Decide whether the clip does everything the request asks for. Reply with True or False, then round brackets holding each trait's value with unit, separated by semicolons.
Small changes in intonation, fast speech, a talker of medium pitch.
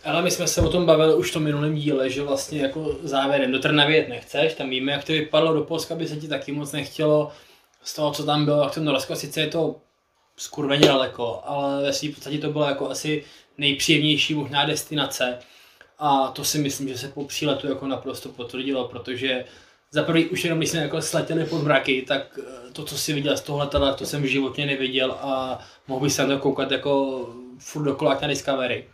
True (2.0 semitones; 210 wpm; 145 Hz)